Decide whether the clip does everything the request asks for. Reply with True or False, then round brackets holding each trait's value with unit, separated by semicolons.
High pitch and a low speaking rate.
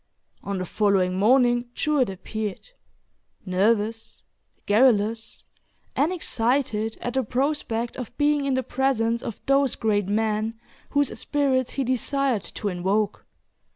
True (230 Hz; 120 wpm)